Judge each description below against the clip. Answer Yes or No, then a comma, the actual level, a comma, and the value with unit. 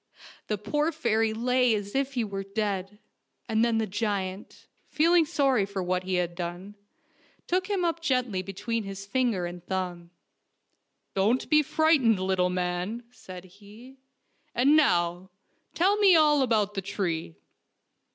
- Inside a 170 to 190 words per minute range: No, average, 150 wpm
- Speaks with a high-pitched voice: Yes, high, 210 Hz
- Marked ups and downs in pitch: Yes, wide, 5.7 semitones